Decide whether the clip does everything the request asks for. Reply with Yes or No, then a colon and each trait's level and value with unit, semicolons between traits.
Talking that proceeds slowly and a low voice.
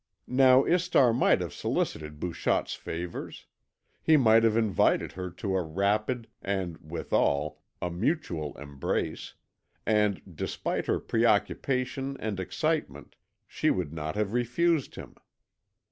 Yes: slow, 120 wpm; low, 100 Hz